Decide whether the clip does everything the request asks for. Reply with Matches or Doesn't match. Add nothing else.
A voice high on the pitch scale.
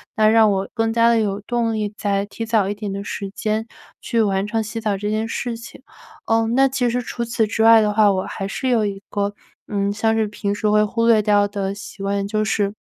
Matches